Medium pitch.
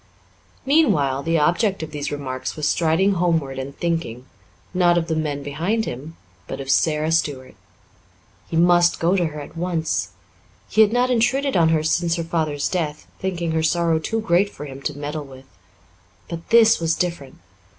Yes: medium, 165 Hz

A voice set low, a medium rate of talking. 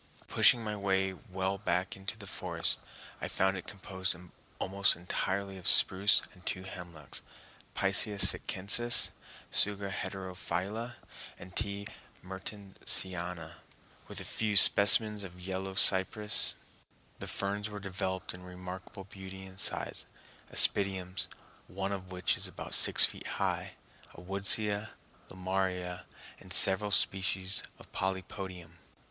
No: very low, 95 Hz; slow, 120 wpm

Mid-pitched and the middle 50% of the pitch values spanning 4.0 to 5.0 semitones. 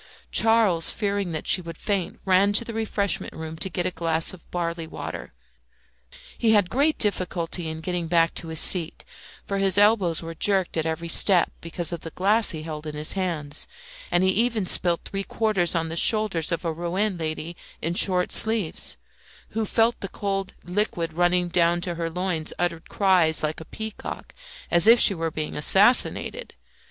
No: medium, 175 Hz; average, 3.4 semitones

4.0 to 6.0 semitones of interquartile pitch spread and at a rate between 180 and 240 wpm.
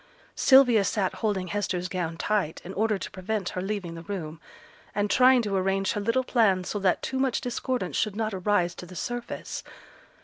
No: average, 3.5 semitones; average, 190 wpm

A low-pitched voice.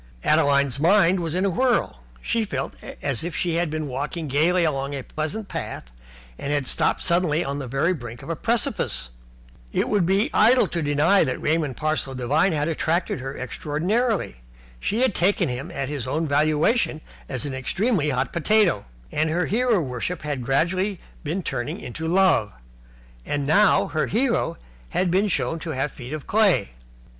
No: medium, 155 Hz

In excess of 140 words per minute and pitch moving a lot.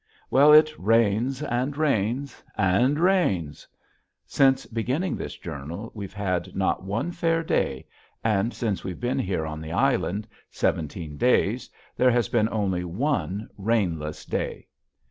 No: slow, 135 wpm; wide, 6.3 semitones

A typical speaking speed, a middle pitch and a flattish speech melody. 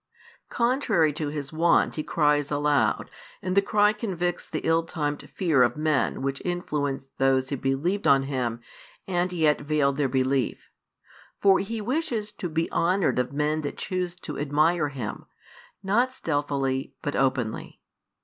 No: average, 155 wpm; medium, 150 Hz; average, 4.6 semitones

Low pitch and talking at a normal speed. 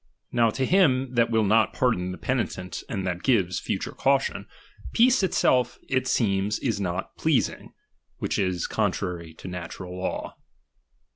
Yes: low, 105 Hz; average, 155 wpm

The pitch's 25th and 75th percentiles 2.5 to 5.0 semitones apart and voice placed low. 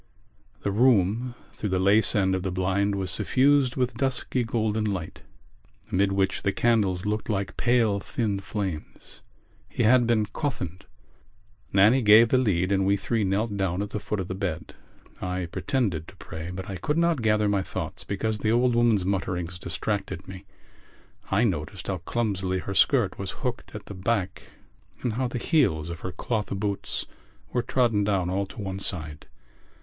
Yes: average, 3.6 semitones; low, 100 Hz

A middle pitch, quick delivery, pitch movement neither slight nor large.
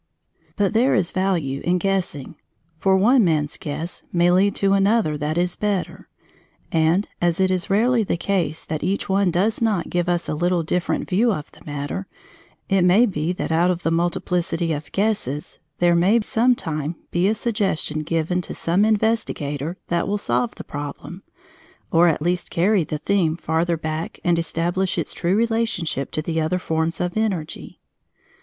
No: medium, 175 Hz; average, 175 wpm; average, 3.6 semitones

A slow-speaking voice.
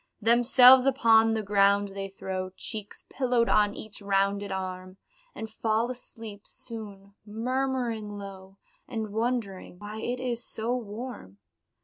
Yes: slow, 125 wpm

